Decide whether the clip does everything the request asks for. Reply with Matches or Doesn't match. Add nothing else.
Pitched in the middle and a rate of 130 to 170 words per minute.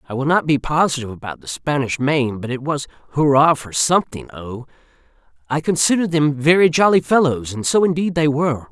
Doesn't match